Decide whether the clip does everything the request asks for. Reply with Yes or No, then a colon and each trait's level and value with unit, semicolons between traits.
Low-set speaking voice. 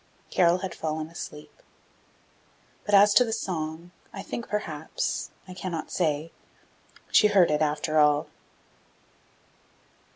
No: medium, 170 Hz